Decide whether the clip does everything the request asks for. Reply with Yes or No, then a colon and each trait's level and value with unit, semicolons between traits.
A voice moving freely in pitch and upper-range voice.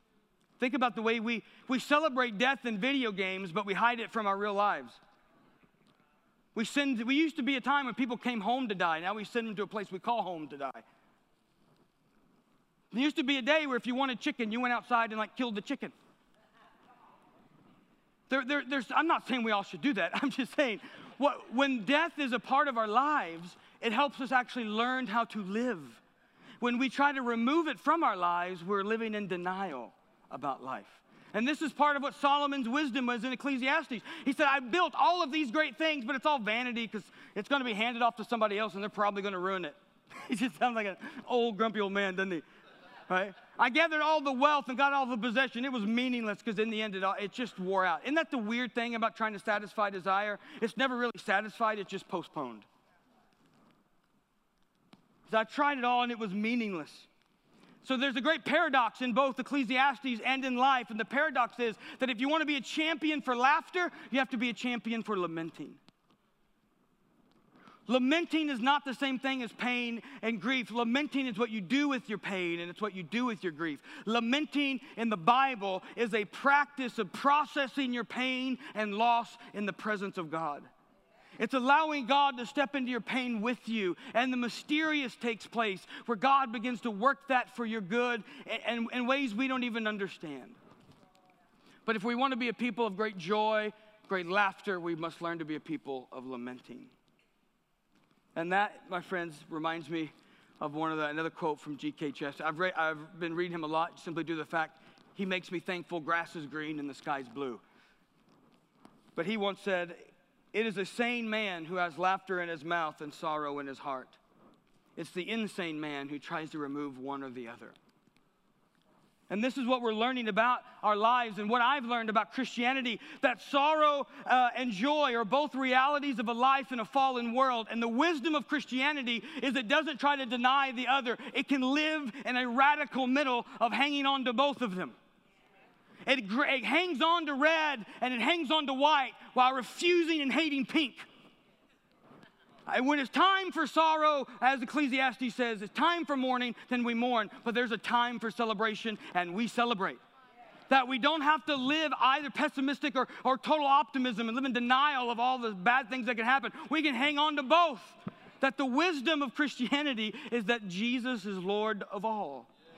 No: average, 4.7 semitones; high, 240 Hz